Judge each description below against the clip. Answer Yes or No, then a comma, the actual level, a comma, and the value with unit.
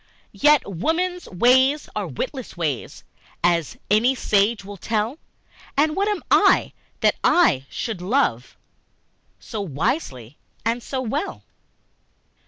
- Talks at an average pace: No, slow, 115 wpm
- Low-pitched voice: No, high, 230 Hz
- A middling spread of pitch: No, wide, 8.8 semitones